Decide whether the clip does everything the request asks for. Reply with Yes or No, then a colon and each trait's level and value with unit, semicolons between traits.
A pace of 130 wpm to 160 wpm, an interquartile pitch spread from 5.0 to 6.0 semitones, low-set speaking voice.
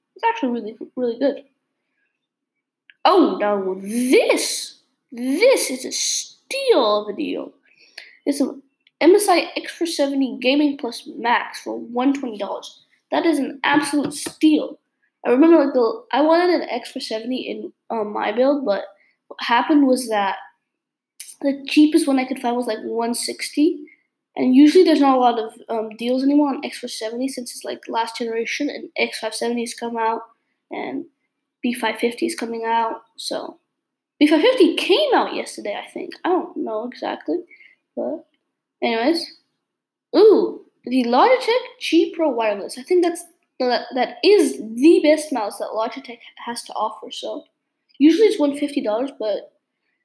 No: average, 150 wpm; average, 5.3 semitones; very high, 285 Hz